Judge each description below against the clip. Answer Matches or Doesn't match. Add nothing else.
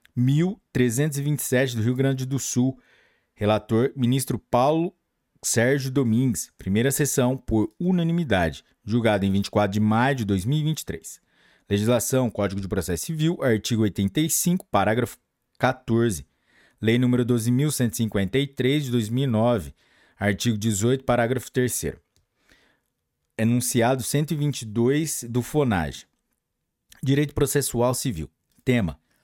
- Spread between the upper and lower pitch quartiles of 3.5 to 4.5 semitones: Matches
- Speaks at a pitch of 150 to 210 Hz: Doesn't match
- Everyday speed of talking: Doesn't match